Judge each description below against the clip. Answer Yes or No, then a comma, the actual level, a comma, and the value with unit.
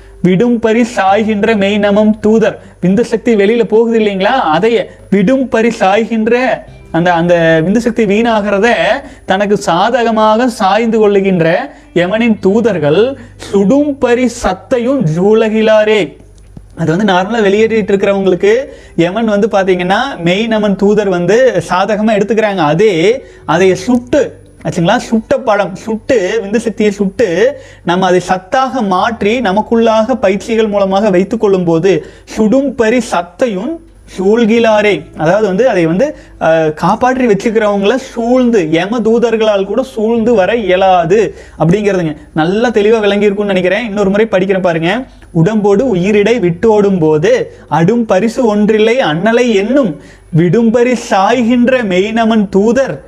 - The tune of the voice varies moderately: Yes, average, 3.4 semitones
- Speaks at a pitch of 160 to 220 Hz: Yes, high, 215 Hz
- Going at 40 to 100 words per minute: No, average, 115 wpm